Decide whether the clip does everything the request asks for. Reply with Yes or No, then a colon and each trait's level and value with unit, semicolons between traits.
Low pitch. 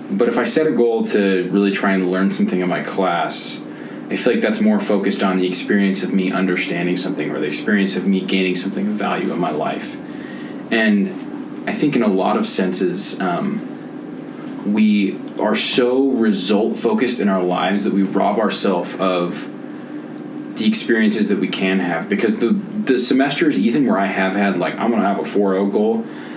Yes: low, 100 Hz